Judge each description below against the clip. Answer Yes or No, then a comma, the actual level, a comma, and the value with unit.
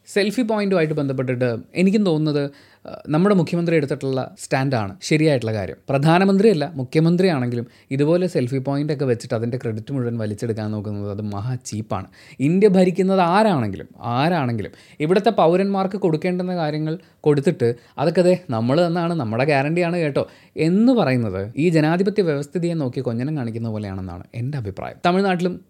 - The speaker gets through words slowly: No, fast, 125 wpm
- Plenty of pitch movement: Yes, wide, 6.9 semitones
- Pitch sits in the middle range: Yes, medium, 145 Hz